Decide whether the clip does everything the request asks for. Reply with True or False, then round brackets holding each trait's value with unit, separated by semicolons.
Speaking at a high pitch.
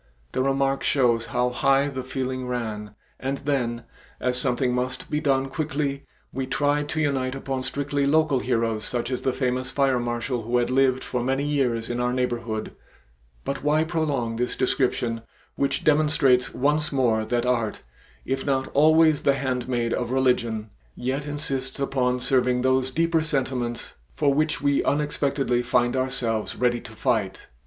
False (130 Hz)